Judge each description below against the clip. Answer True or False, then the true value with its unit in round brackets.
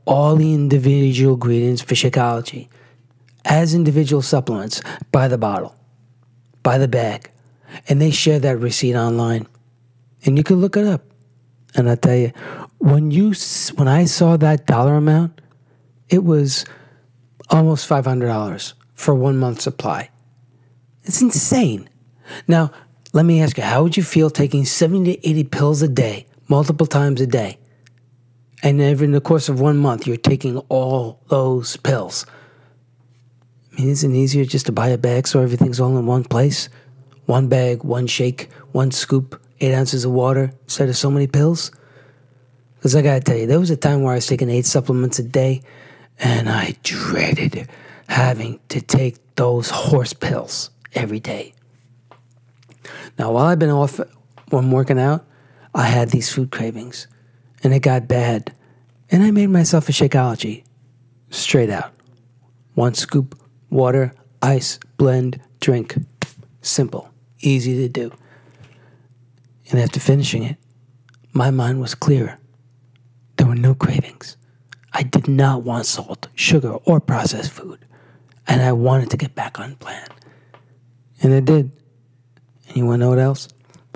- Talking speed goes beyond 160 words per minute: False (150 wpm)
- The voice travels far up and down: False (2.6 semitones)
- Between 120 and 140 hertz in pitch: True (130 Hz)